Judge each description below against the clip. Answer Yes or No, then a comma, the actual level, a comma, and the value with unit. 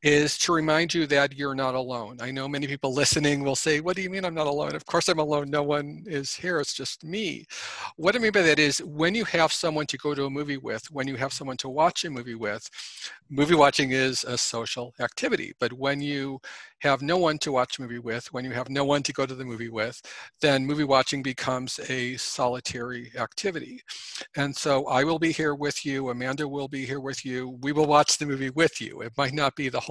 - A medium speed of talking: No, fast, 240 wpm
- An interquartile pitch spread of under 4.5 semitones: Yes, narrow, 2.6 semitones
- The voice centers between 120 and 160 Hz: Yes, medium, 140 Hz